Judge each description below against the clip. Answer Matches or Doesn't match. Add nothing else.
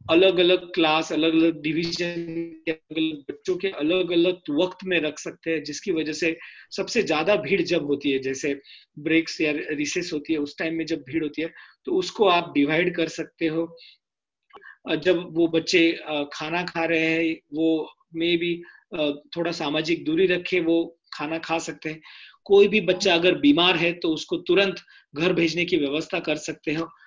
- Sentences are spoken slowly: Doesn't match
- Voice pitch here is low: Doesn't match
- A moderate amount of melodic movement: Doesn't match